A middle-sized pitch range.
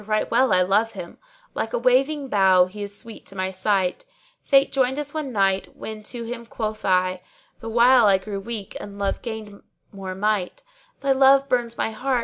Yes: average, 4.6 semitones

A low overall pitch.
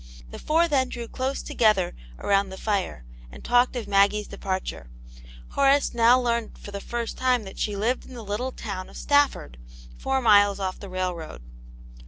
No: high, 215 Hz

